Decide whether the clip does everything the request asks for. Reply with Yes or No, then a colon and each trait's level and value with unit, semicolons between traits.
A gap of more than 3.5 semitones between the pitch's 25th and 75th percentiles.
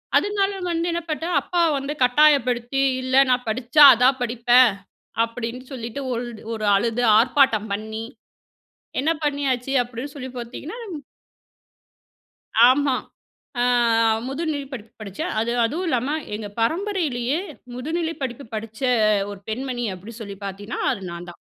Yes: average, 3.9 semitones